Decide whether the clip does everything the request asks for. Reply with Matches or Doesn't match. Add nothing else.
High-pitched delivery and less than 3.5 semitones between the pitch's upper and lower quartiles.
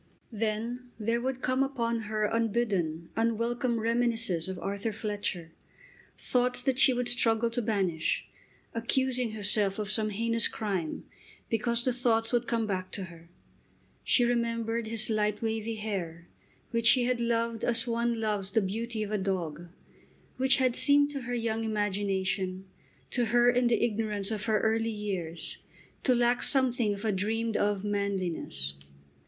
Matches